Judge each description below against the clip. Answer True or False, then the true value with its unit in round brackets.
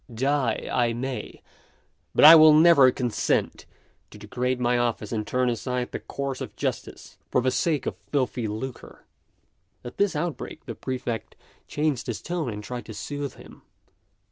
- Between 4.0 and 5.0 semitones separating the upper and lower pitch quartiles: False (3.3 semitones)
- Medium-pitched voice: False (125 Hz)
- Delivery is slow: False (160 wpm)